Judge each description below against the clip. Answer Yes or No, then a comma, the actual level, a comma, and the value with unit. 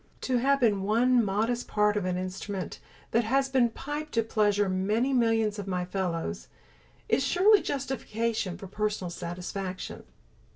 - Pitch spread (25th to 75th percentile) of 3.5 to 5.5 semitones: Yes, average, 4.5 semitones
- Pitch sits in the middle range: No, high, 210 Hz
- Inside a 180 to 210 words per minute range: No, average, 140 wpm